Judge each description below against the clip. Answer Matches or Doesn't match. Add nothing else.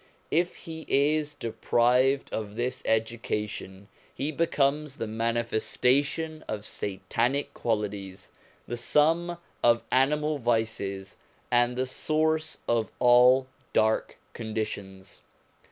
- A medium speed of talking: Doesn't match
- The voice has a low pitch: Matches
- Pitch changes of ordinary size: Matches